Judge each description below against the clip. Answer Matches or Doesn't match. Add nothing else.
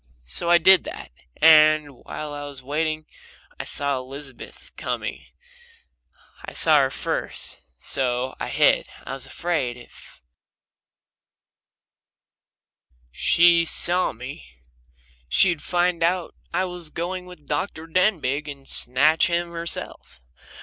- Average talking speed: Doesn't match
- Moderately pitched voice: Matches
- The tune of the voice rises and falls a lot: Doesn't match